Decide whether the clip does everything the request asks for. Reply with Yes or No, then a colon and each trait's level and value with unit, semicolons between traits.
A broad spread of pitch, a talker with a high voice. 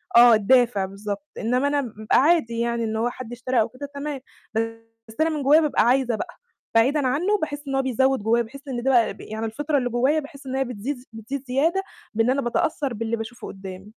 No: average, 3.8 semitones; very high, 250 Hz